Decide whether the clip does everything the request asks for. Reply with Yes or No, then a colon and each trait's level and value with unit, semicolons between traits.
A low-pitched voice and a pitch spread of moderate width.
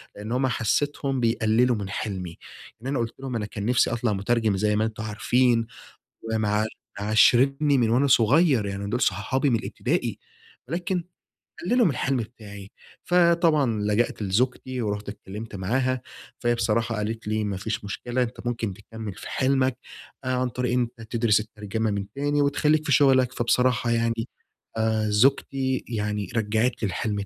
Yes: low, 115 Hz; average, 3.4 semitones